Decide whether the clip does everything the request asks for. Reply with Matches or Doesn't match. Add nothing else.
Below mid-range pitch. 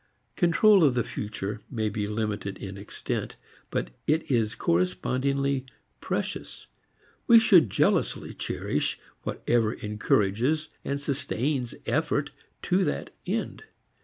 Matches